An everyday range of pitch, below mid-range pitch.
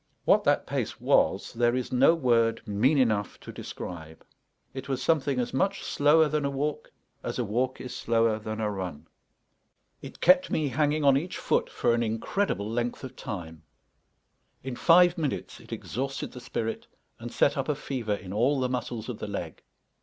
Yes: average, 4.5 semitones; low, 125 Hz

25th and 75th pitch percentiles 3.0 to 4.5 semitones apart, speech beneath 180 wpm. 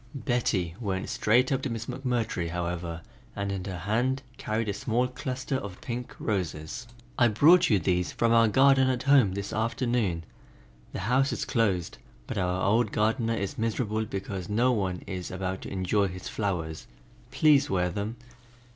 No: average, 5.0 semitones; average, 165 wpm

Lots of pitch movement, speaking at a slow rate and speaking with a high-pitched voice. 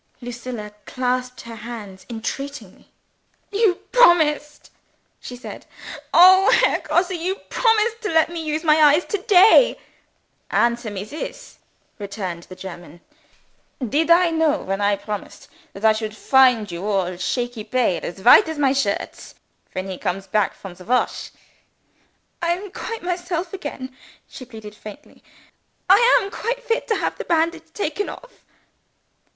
No: wide, 8.8 semitones; average, 145 wpm; very high, 260 Hz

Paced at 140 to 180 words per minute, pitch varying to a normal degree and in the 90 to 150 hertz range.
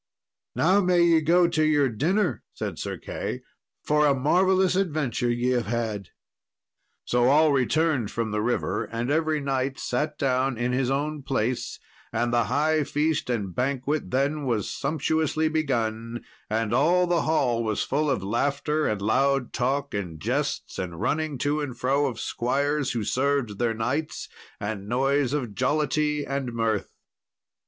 Yes: average, 155 wpm; average, 4.3 semitones; low, 135 Hz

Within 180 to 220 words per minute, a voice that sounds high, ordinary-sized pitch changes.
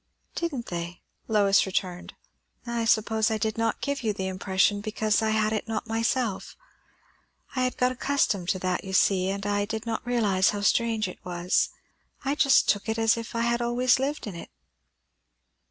Yes: average, 185 wpm; high, 220 Hz; average, 3.2 semitones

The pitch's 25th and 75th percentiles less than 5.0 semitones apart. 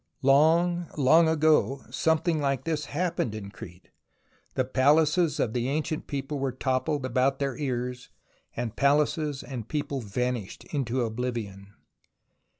Yes: average, 3.6 semitones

